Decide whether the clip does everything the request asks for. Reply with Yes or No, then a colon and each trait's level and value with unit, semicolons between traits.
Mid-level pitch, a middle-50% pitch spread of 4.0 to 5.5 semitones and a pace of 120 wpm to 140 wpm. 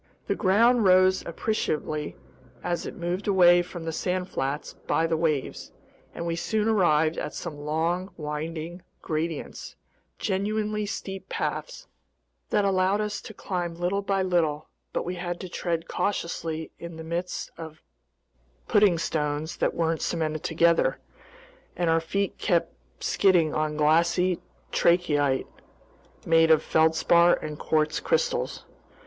No: medium, 170 Hz; average, 2.8 semitones; slow, 135 wpm